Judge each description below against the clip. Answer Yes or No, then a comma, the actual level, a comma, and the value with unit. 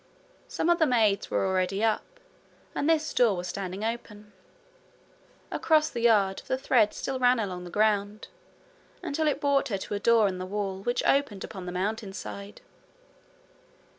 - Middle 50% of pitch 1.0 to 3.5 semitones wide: No, average, 4.5 semitones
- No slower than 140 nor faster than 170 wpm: Yes, average, 165 wpm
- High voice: Yes, high, 215 Hz